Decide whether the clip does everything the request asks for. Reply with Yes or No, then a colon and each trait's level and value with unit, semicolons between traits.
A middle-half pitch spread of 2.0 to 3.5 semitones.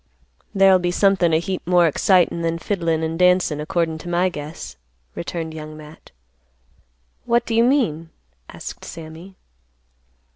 Yes: narrow, 2.6 semitones